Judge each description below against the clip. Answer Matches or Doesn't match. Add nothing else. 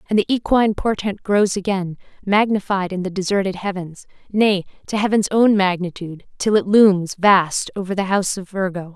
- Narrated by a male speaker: Doesn't match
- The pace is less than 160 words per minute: Doesn't match